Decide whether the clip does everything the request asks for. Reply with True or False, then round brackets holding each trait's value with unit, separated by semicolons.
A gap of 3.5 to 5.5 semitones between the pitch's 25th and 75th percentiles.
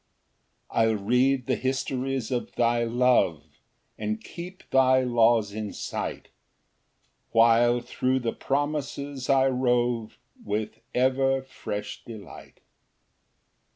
False (2.6 semitones)